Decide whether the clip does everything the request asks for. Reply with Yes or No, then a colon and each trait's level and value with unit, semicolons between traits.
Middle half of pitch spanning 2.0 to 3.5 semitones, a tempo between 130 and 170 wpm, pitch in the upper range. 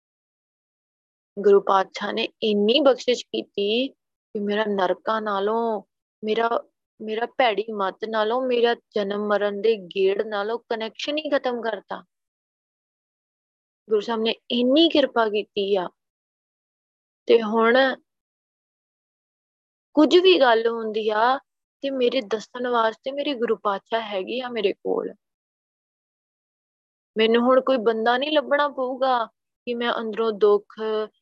No: average, 3.1 semitones; average, 115 wpm; high, 225 Hz